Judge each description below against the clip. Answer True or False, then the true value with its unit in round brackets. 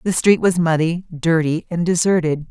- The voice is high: False (170 Hz)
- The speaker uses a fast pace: False (170 wpm)